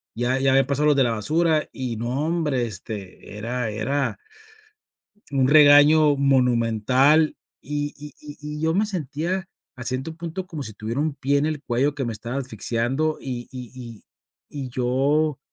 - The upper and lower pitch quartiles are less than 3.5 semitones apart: No, average, 3.8 semitones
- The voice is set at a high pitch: No, low, 135 Hz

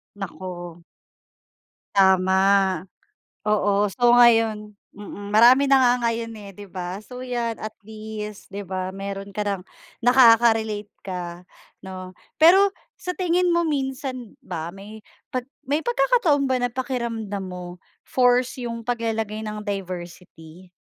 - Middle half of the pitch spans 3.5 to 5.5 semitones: Yes, average, 4.1 semitones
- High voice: Yes, high, 215 Hz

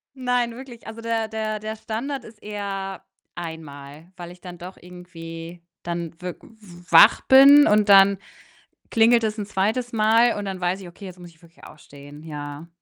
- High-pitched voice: Yes, high, 195 Hz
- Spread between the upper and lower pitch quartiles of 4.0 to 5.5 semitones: Yes, average, 4.7 semitones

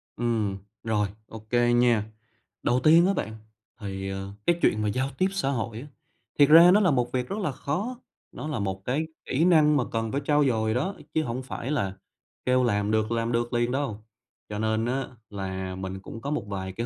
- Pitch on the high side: No, low, 120 Hz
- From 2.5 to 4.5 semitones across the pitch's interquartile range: No, average, 5.3 semitones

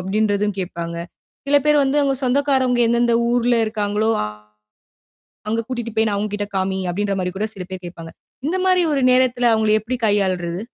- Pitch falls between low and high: No, high, 220 Hz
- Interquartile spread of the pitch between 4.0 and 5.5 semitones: Yes, average, 4.3 semitones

